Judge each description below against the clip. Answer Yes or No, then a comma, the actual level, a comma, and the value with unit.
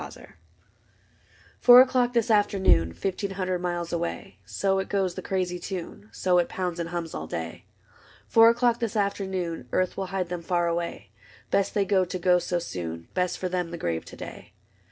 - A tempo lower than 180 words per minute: No, average, 185 wpm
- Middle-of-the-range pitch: Yes, medium, 180 Hz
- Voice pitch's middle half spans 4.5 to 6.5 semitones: No, narrow, 2.5 semitones